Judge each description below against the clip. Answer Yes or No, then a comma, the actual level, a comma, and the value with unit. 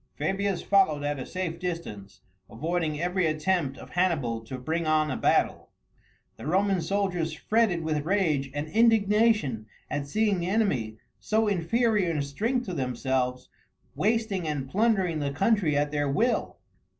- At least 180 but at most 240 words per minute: No, average, 150 wpm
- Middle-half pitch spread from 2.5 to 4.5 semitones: No, wide, 5.6 semitones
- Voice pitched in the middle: Yes, medium, 170 Hz